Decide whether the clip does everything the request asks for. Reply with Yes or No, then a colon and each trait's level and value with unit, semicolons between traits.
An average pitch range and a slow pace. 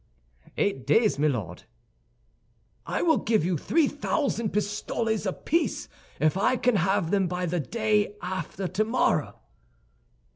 Yes: average, 4.0 semitones; slow, 125 wpm